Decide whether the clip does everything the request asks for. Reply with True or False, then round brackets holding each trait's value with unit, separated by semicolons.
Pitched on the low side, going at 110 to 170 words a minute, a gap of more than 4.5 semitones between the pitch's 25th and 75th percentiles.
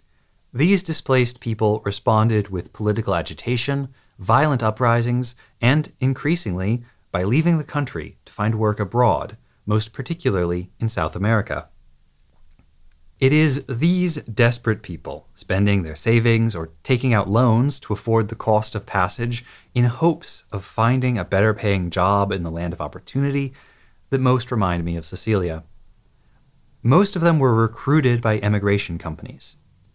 True (110 Hz; 140 wpm; 5.0 semitones)